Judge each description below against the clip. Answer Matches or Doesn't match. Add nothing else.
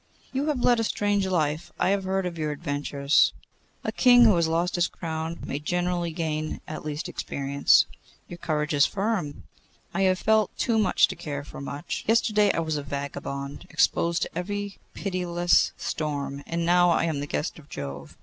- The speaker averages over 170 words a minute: Matches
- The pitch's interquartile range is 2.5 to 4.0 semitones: Doesn't match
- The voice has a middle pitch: Matches